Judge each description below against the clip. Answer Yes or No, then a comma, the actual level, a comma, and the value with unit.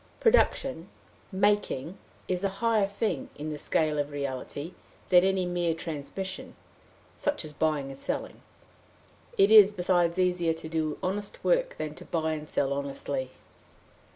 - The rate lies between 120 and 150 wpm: Yes, average, 145 wpm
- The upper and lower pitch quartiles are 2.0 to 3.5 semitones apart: No, average, 4.4 semitones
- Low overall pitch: No, medium, 170 Hz